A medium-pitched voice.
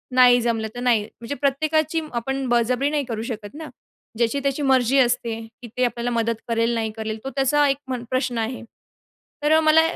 No: high, 245 Hz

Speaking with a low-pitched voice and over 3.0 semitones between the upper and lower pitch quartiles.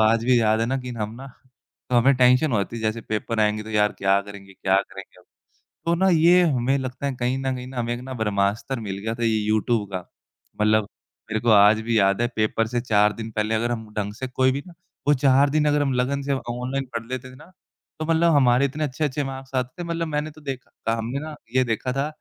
Yes: low, 120 Hz; average, 3.8 semitones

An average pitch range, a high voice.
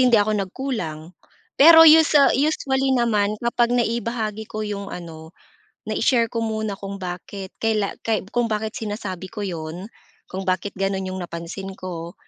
Yes: average, 3.9 semitones; high, 210 Hz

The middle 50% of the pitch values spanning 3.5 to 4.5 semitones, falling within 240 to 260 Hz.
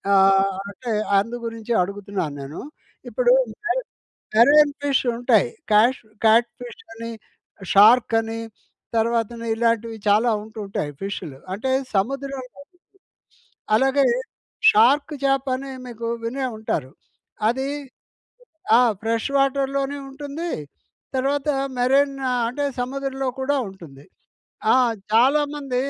Yes: average, 3.8 semitones; high, 245 Hz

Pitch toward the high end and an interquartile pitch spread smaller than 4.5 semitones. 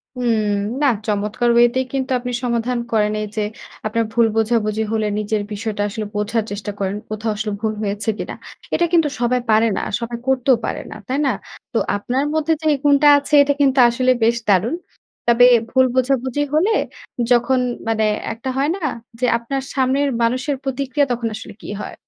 Yes: high, 240 Hz; average, 3.4 semitones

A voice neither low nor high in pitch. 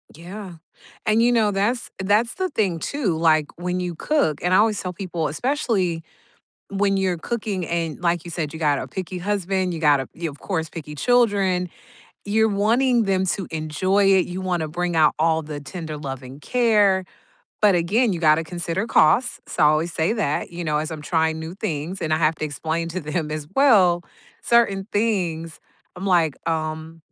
Yes: medium, 175 Hz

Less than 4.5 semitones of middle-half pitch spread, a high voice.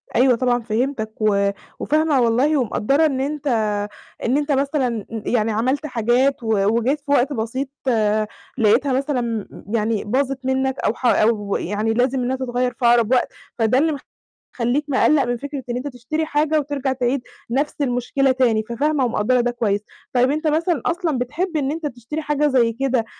Yes: average, 3.5 semitones; very high, 255 Hz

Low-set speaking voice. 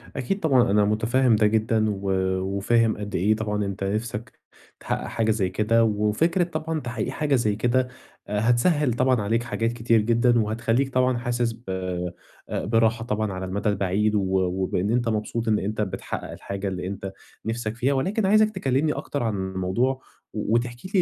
Yes: low, 115 Hz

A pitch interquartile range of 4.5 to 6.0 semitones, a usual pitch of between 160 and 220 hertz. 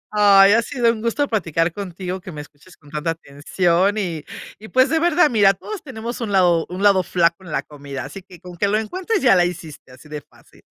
Yes: average, 4.9 semitones; high, 190 Hz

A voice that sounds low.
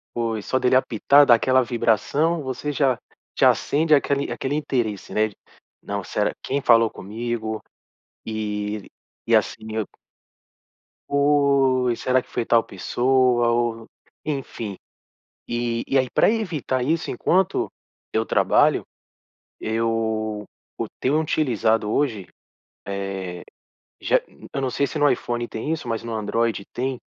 Yes: low, 120 Hz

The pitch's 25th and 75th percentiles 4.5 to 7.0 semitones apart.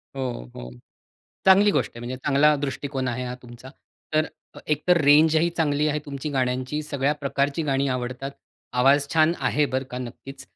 No: average, 2.8 semitones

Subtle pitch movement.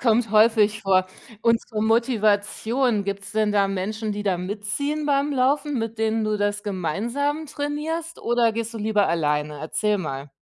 No: average, 3.1 semitones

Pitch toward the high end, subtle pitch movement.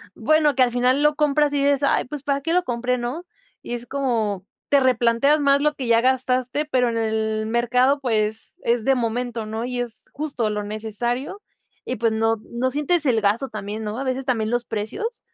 No: high, 245 Hz; average, 3.8 semitones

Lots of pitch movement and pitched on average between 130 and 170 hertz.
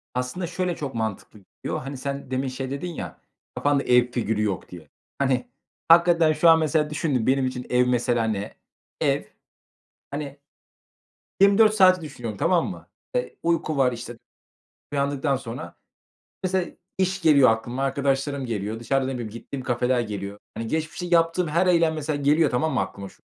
No: average, 4.9 semitones; low, 135 Hz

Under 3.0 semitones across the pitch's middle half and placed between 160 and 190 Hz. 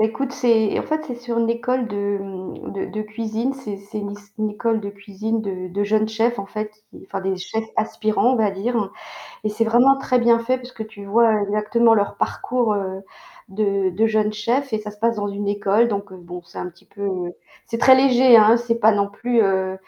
No: narrow, 2.5 semitones; high, 215 Hz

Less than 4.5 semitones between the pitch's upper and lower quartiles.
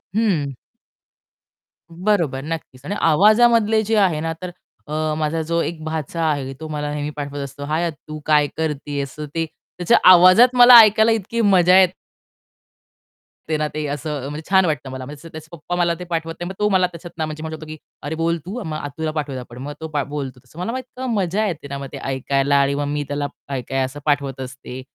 Yes: average, 3.9 semitones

